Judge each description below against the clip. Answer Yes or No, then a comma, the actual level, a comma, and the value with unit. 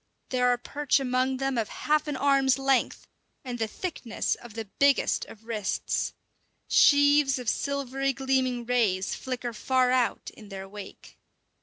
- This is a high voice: Yes, very high, 255 Hz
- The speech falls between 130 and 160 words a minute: Yes, average, 150 wpm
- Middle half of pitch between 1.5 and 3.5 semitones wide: Yes, average, 2.7 semitones